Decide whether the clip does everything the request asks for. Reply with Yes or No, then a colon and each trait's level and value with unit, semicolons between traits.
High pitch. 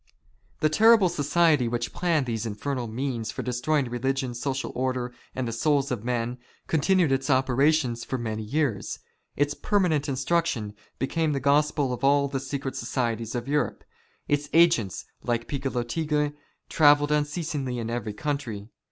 No: low, 135 Hz